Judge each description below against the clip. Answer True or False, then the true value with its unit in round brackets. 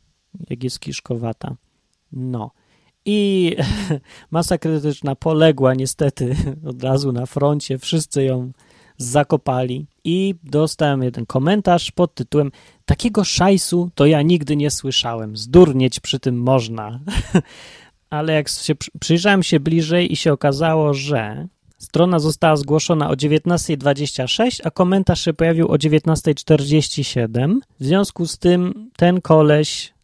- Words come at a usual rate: True (120 wpm)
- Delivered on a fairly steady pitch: False (4.1 semitones)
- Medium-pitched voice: True (150 Hz)